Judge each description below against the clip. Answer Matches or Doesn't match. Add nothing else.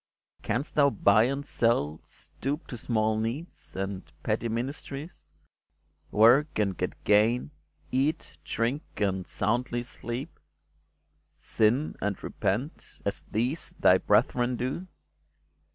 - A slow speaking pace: Matches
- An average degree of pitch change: Matches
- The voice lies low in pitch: Matches